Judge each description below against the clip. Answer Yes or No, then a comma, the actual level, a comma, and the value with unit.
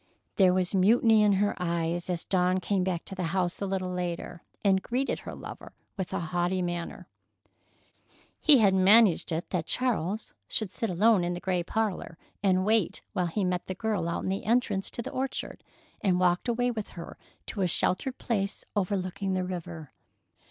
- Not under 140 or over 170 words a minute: No, average, 185 wpm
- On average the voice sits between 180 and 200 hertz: Yes, medium, 185 Hz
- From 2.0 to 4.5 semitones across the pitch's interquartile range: Yes, average, 2.9 semitones